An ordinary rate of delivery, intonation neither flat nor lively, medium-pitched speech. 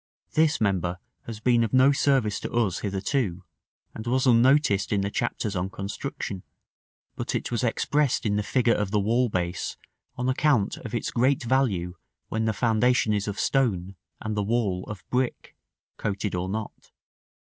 No: average, 170 wpm; average, 4.1 semitones; low, 110 Hz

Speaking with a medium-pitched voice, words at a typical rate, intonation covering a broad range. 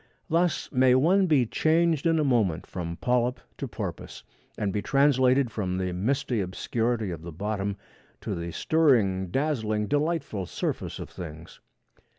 No: low, 120 Hz; average, 150 wpm; wide, 7.4 semitones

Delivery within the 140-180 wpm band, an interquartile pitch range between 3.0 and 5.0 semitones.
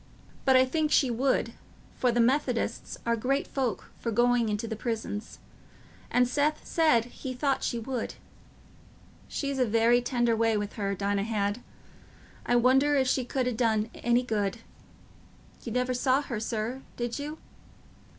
No: average, 160 wpm; narrow, 2.5 semitones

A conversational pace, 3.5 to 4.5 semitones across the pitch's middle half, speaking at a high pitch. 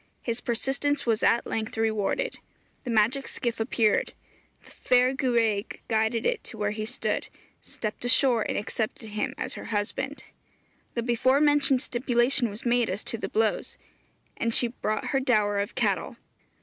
No: average, 160 wpm; average, 3.0 semitones; high, 235 Hz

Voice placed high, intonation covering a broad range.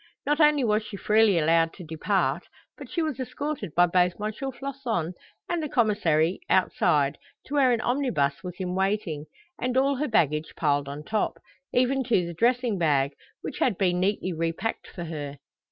Yes: high, 195 Hz; wide, 7.3 semitones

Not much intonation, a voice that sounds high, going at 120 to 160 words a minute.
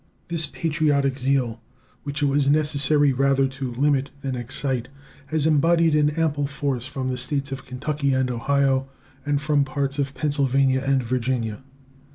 No: narrow, 1.8 semitones; medium, 140 Hz; average, 155 wpm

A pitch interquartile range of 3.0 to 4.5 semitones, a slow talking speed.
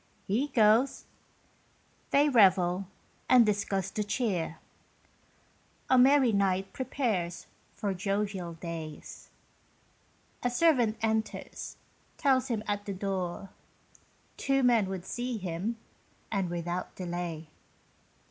No: average, 5.0 semitones; slow, 100 wpm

